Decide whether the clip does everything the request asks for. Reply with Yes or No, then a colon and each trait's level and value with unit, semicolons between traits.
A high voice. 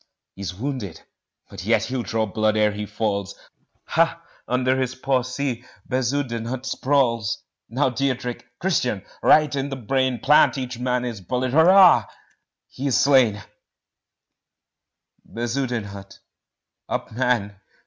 No: low, 125 Hz